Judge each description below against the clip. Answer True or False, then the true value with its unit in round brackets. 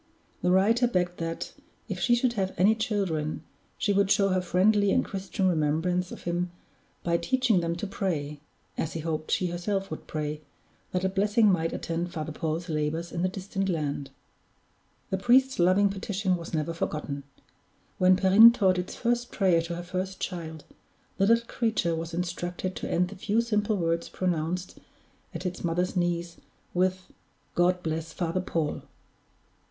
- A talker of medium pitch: True (180 Hz)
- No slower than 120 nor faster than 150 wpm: False (165 wpm)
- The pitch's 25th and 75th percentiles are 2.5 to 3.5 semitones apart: True (2.8 semitones)